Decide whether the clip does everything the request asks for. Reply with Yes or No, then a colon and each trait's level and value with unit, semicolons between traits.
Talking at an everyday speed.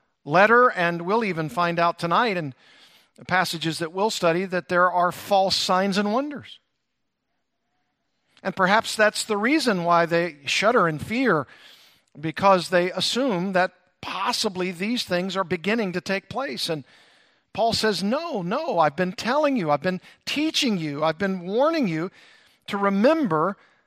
Yes: average, 155 wpm